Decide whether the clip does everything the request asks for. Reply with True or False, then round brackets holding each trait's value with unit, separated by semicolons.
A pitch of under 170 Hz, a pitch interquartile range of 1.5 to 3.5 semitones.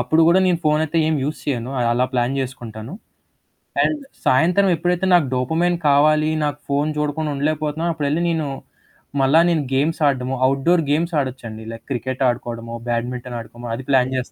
False (140 Hz; 4.0 semitones)